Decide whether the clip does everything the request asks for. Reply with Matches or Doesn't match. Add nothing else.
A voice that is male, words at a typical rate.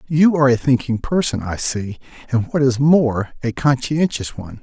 Matches